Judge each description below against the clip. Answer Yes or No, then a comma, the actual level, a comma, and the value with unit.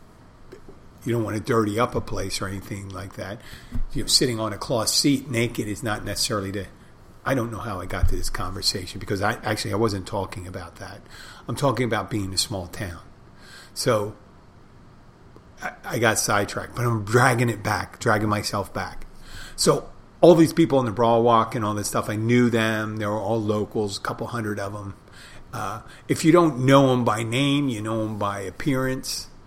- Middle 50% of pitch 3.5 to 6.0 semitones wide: No, average, 3.1 semitones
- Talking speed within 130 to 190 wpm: No, average, 200 wpm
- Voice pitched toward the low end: Yes, low, 110 Hz